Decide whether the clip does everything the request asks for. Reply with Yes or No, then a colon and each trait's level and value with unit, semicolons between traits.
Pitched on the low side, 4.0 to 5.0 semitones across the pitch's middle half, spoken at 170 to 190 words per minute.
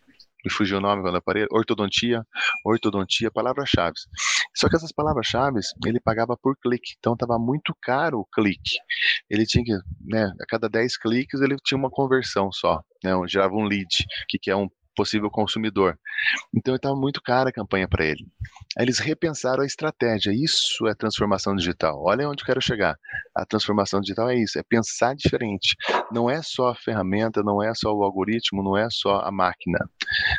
Yes: low, 115 Hz; average, 4.4 semitones; average, 180 wpm